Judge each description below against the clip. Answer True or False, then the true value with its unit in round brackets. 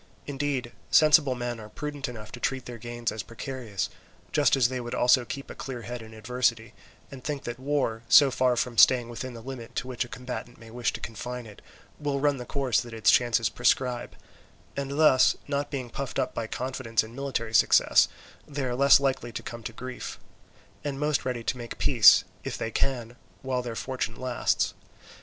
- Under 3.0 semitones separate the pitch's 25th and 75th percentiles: True (2.5 semitones)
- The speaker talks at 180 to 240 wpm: True (195 wpm)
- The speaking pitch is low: True (125 Hz)